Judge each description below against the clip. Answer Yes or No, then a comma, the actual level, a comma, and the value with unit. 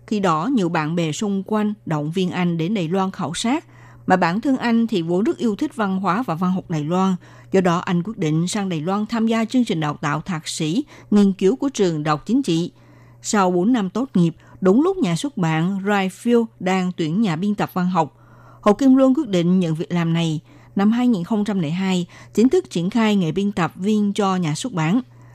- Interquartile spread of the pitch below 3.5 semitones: No, average, 4.2 semitones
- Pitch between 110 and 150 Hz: No, high, 190 Hz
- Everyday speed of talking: Yes, average, 225 wpm